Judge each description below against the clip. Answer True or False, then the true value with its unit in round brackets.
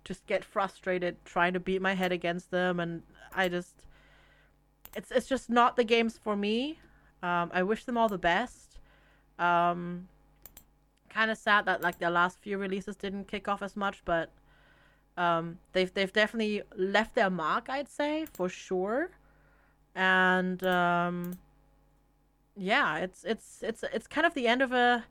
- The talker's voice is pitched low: False (185 Hz)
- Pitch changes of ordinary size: True (3.8 semitones)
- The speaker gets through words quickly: False (165 wpm)